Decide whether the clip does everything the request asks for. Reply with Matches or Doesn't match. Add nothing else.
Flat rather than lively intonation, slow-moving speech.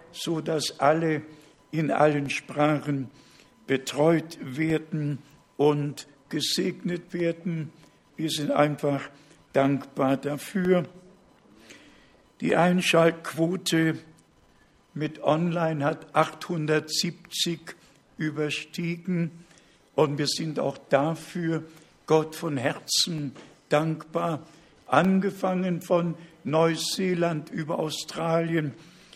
Matches